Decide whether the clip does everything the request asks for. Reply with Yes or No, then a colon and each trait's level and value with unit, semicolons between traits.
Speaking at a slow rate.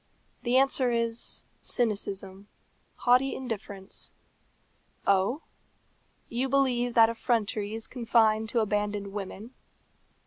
Yes: slow, 95 wpm